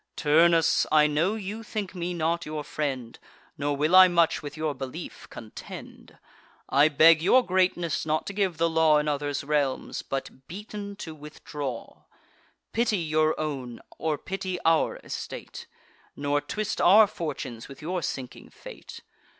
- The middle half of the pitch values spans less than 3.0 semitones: No, average, 3.7 semitones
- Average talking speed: Yes, average, 150 wpm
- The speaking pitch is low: No, medium, 155 Hz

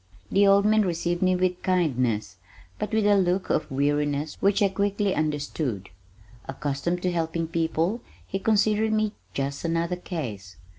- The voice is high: No, medium, 175 Hz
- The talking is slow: No, average, 150 wpm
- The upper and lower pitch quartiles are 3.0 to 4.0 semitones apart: No, average, 5.2 semitones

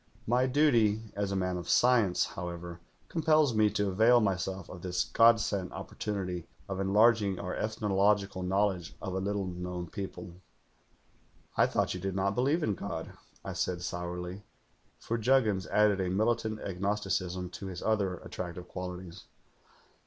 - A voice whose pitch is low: Yes, very low, 95 Hz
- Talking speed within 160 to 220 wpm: No, average, 150 wpm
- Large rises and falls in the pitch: No, average, 3.1 semitones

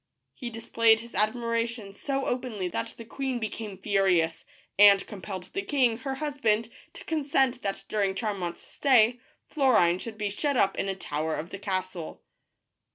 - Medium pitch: No, high, 220 Hz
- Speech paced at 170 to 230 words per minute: No, average, 160 wpm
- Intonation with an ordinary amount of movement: Yes, average, 4.2 semitones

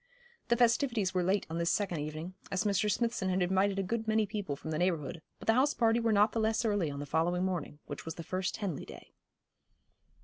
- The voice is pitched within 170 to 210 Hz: Yes, high, 190 Hz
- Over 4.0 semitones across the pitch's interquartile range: Yes, average, 4.5 semitones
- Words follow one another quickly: Yes, fast, 230 wpm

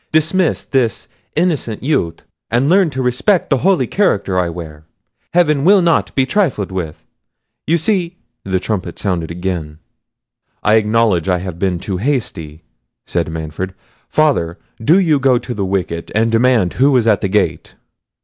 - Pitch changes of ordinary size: No, wide, 8.6 semitones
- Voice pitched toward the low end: Yes, low, 110 Hz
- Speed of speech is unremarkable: Yes, average, 160 wpm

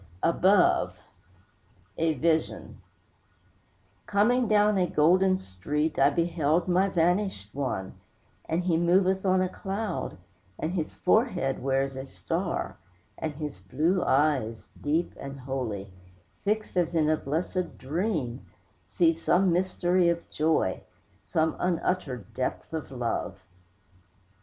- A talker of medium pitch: Yes, medium, 165 Hz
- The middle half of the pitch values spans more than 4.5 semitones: Yes, average, 5.2 semitones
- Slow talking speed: Yes, slow, 120 wpm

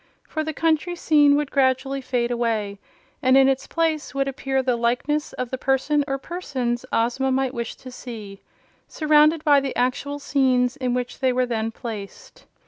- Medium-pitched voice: No, very high, 265 Hz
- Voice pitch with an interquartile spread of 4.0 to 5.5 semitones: No, average, 2.9 semitones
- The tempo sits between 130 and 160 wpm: No, average, 175 wpm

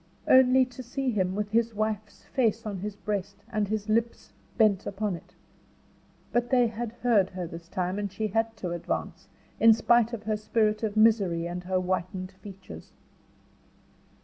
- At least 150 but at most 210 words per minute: Yes, average, 170 wpm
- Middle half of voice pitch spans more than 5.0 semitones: No, average, 3.2 semitones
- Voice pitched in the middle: No, high, 210 Hz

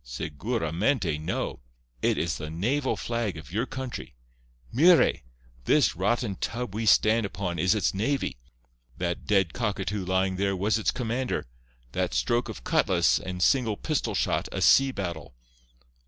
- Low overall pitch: Yes, very low, 95 Hz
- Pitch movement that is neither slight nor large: No, wide, 6.4 semitones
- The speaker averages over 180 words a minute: No, average, 140 wpm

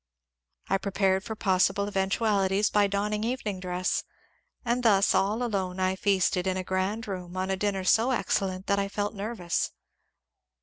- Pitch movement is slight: Yes, narrow, 1.9 semitones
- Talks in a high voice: Yes, high, 195 Hz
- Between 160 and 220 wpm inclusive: Yes, average, 170 wpm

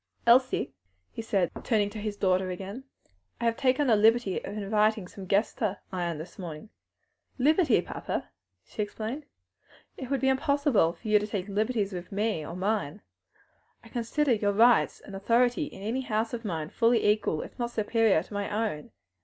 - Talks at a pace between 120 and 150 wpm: No, average, 180 wpm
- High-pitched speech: Yes, high, 215 Hz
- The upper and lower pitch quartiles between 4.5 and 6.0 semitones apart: No, average, 3.5 semitones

